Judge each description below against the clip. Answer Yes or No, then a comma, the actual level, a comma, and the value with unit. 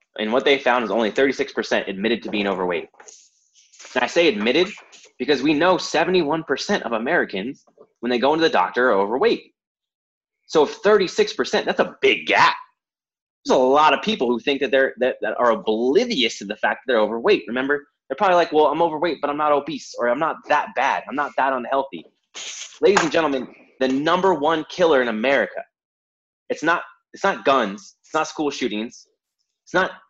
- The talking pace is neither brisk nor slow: Yes, average, 185 wpm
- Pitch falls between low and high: Yes, medium, 160 Hz